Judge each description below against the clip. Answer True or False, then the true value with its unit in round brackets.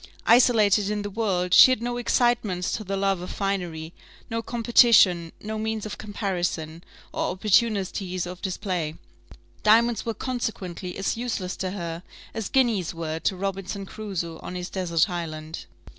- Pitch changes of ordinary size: True (3.7 semitones)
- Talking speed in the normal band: True (150 wpm)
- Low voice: False (195 Hz)